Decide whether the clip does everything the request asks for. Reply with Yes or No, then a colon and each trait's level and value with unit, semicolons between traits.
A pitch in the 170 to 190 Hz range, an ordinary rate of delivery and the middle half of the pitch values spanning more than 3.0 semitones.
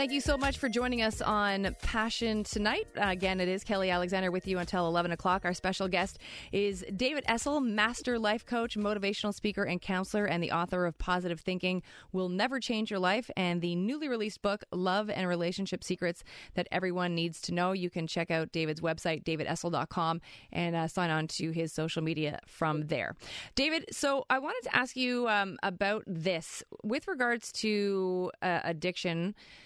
Yes: medium, 185 Hz; average, 180 wpm; average, 3.5 semitones